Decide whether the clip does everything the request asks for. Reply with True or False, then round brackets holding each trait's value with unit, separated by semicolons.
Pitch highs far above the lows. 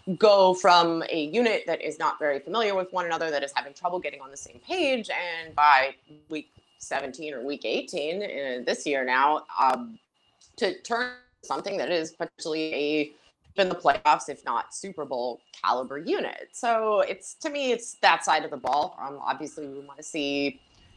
True (7.2 semitones)